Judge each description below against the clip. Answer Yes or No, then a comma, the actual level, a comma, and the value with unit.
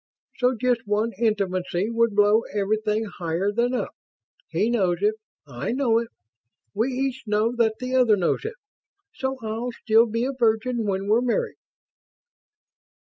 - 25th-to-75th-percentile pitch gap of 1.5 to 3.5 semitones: Yes, average, 2.9 semitones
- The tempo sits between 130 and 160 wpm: Yes, average, 150 wpm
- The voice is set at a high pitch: Yes, high, 225 Hz